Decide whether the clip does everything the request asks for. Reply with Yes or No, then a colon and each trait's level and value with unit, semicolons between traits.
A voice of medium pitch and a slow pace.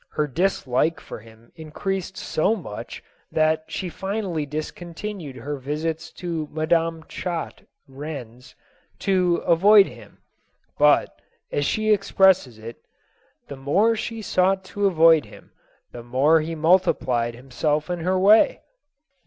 Yes: medium, 160 Hz; slow, 130 wpm